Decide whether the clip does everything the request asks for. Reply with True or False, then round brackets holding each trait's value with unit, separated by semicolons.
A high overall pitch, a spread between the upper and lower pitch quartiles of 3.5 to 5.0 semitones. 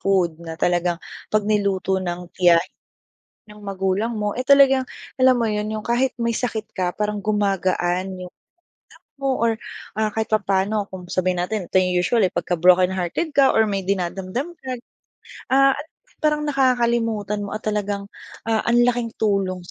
True (205 Hz; 4.0 semitones)